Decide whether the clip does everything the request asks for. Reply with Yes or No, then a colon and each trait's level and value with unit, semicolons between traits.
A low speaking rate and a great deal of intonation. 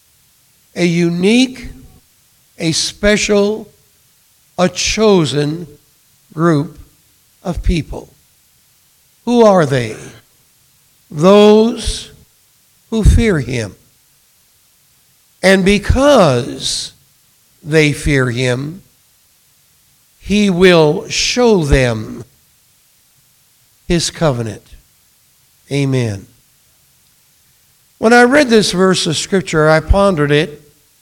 Yes: slow, 75 wpm; wide, 6.5 semitones